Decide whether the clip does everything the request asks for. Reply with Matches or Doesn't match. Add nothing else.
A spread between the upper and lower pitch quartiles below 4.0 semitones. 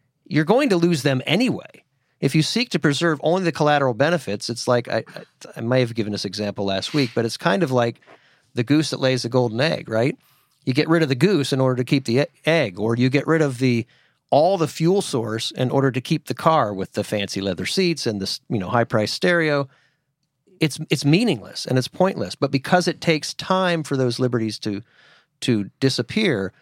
Doesn't match